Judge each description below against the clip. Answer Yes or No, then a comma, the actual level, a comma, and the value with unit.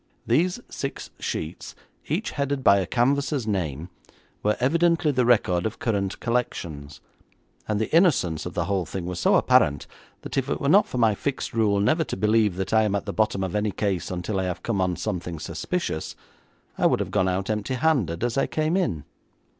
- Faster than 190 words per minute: Yes, average, 200 wpm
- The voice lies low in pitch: Yes, low, 105 Hz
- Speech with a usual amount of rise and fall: No, wide, 6.2 semitones